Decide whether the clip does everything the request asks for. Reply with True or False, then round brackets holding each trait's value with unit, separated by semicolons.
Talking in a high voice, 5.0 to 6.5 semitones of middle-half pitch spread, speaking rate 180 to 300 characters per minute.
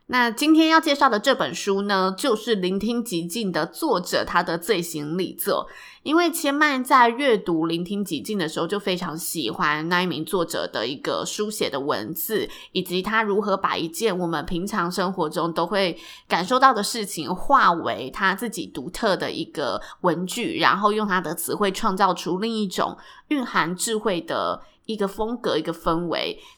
True (200 Hz; 5.5 semitones; 270 characters per minute)